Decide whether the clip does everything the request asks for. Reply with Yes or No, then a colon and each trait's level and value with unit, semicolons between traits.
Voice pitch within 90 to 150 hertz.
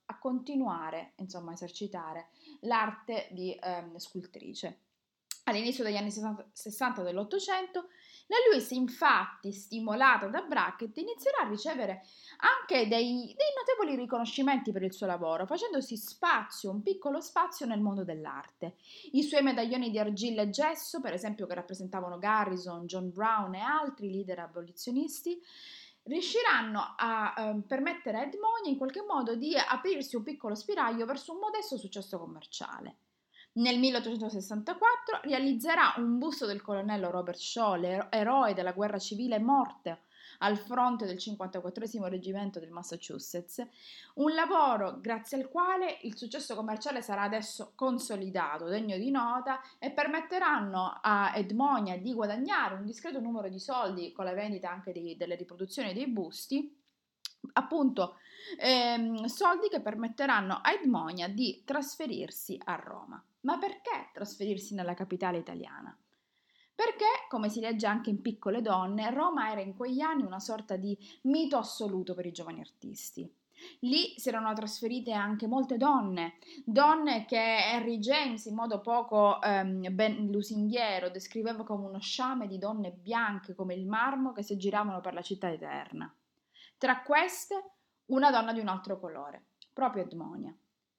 No: high, 225 Hz